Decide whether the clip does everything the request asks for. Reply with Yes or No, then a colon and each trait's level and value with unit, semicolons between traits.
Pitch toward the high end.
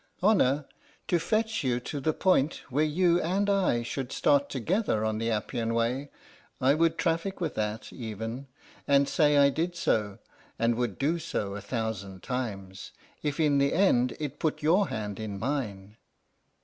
No: low, 135 Hz